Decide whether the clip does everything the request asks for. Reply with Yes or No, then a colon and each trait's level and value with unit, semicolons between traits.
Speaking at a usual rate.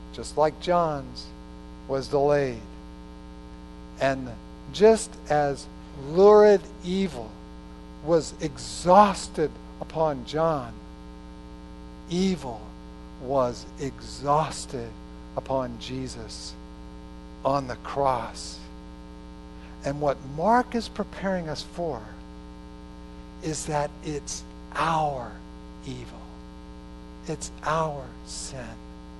No: slow, 75 wpm